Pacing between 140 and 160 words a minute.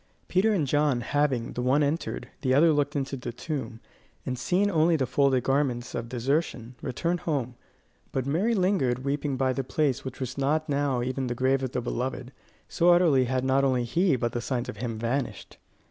No: average, 195 wpm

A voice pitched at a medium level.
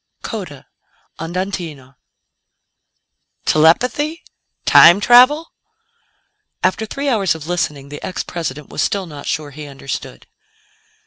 Yes: medium, 170 Hz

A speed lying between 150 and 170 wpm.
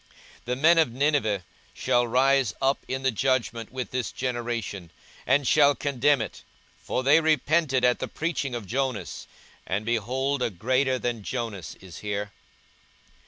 Yes: average, 155 wpm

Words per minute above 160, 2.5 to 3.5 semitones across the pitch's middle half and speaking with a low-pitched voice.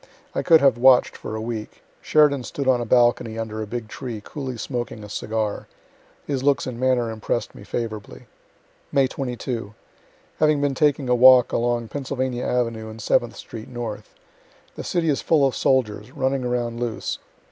Yes: average, 170 wpm; average, 2.8 semitones; low, 120 Hz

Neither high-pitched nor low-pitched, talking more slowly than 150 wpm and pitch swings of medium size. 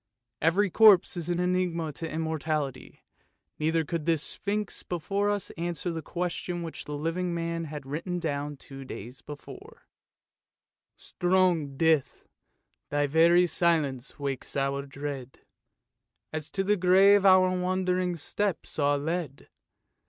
Yes: medium, 165 Hz; slow, 135 wpm; average, 3.7 semitones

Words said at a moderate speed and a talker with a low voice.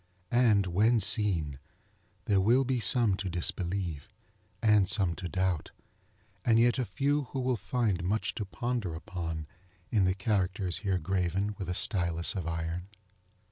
Yes: average, 150 wpm; very low, 95 Hz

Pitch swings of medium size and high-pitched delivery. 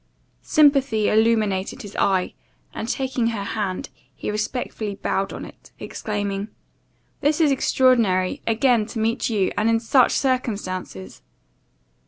Yes: average, 4.0 semitones; high, 220 Hz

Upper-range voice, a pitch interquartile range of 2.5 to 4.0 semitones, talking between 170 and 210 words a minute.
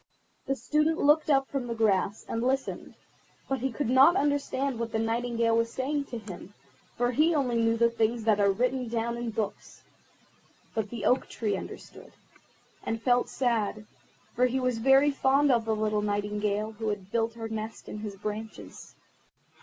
Yes: high, 230 Hz; average, 3.4 semitones; average, 175 wpm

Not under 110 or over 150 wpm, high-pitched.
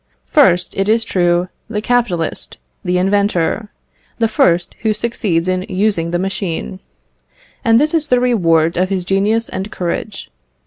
Yes: average, 145 wpm; high, 195 Hz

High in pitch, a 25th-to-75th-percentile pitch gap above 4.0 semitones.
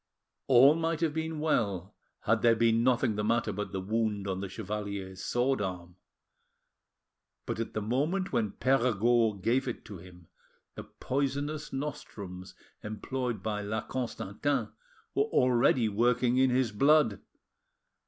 No: low, 115 Hz; average, 4.5 semitones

